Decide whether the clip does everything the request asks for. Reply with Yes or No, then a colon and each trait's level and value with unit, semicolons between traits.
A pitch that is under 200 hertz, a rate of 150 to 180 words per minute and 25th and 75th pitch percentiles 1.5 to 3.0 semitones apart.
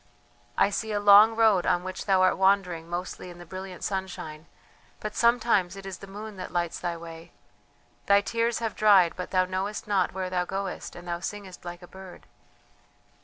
No: high, 190 Hz; average, 190 wpm; narrow, 2.5 semitones